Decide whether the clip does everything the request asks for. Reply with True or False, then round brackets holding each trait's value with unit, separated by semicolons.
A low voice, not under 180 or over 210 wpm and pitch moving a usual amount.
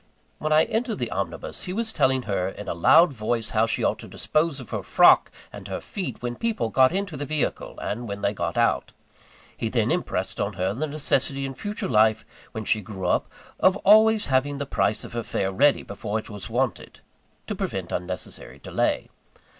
False (125 Hz; 200 wpm; 6.6 semitones)